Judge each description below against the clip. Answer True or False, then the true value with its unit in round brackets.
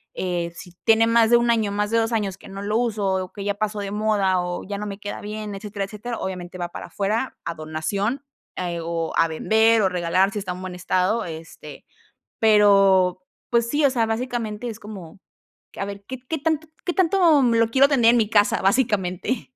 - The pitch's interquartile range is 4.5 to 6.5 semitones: False (3.6 semitones)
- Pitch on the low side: False (210 Hz)